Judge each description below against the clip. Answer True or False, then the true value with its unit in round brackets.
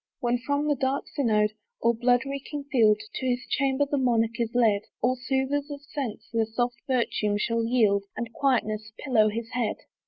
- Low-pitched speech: False (245 Hz)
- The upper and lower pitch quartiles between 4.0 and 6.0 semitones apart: False (3.3 semitones)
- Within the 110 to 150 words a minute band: False (180 wpm)